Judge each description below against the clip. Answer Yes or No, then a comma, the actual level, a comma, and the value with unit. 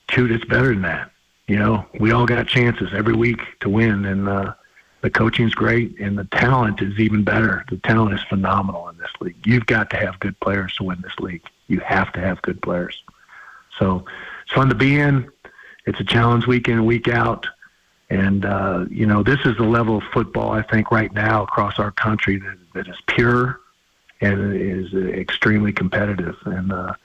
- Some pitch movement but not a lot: Yes, average, 3.1 semitones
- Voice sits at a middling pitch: No, low, 110 Hz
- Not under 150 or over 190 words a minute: No, average, 200 wpm